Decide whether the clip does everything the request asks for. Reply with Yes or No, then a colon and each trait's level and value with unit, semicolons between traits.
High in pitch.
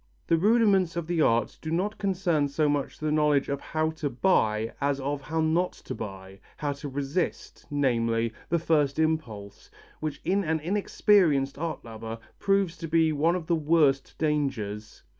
No: medium, 150 Hz